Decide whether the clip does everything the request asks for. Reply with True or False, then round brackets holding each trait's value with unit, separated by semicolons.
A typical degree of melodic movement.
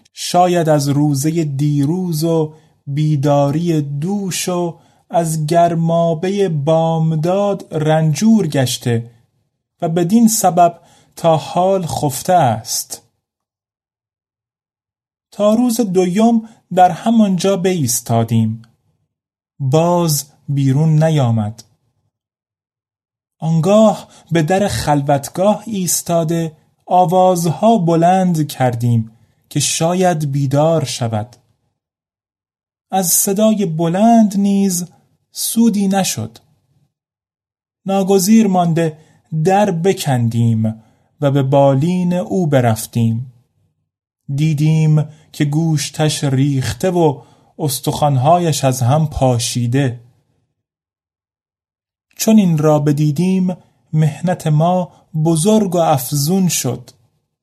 False (6.2 semitones)